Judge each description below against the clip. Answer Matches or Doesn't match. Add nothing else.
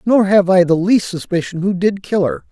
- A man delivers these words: Matches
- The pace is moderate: Doesn't match